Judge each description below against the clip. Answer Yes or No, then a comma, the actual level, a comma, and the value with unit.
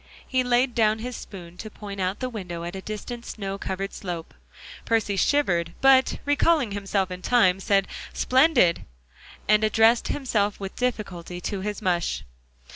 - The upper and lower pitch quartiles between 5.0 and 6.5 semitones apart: No, average, 4.4 semitones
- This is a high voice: Yes, high, 205 Hz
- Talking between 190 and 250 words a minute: No, average, 155 wpm